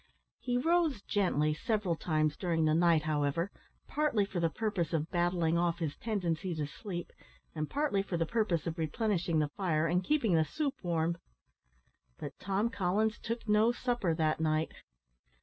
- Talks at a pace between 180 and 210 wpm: No, average, 165 wpm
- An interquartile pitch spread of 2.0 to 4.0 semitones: No, average, 4.9 semitones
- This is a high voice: No, medium, 175 Hz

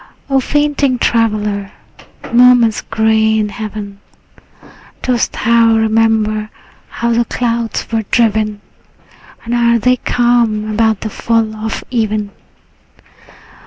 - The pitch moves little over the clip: Yes, narrow, 1.6 semitones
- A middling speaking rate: No, slow, 110 wpm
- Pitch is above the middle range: Yes, high, 225 Hz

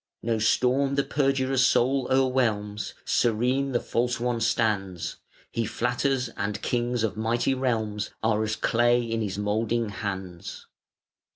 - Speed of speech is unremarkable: No, slow, 130 wpm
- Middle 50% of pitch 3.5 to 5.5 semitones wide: No, average, 3.0 semitones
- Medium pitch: No, low, 115 Hz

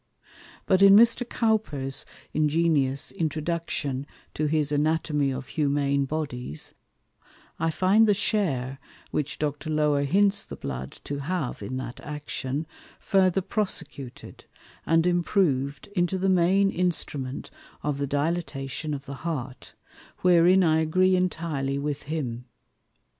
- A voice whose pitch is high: No, medium, 155 Hz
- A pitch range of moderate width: Yes, average, 4.4 semitones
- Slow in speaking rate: Yes, slow, 120 wpm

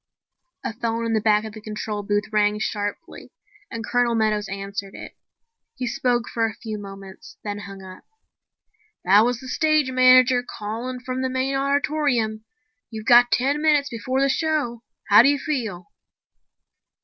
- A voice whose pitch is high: Yes, high, 230 Hz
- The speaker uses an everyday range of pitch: Yes, average, 3.7 semitones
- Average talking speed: Yes, average, 160 wpm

